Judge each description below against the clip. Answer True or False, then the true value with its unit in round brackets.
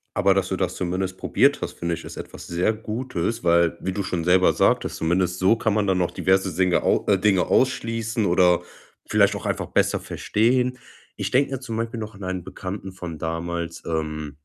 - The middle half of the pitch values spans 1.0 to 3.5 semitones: False (3.9 semitones)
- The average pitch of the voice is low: True (95 Hz)